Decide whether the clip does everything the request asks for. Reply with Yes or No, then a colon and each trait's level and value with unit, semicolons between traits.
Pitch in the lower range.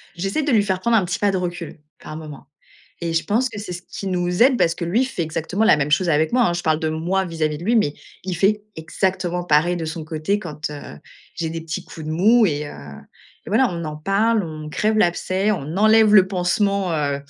No: medium, 175 Hz